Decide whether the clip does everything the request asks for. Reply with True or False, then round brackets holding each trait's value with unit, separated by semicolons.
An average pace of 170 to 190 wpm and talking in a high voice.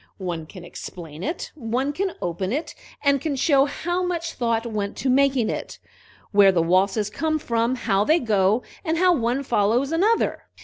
True (175 wpm; 240 Hz)